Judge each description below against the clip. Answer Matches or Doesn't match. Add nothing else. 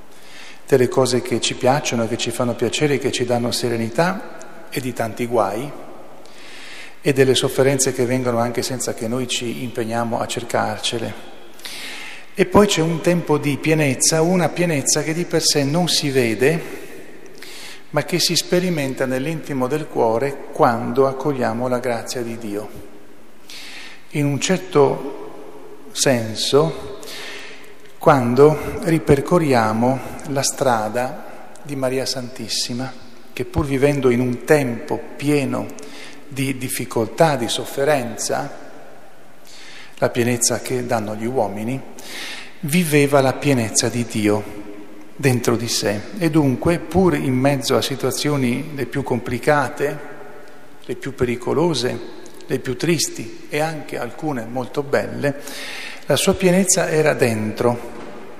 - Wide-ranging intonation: Doesn't match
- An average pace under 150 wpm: Matches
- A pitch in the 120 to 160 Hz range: Matches